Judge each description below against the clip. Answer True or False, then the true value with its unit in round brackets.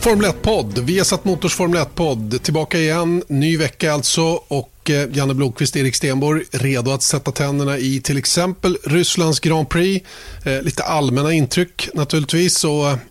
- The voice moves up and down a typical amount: True (3.8 semitones)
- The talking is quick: False (150 wpm)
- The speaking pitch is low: False (155 Hz)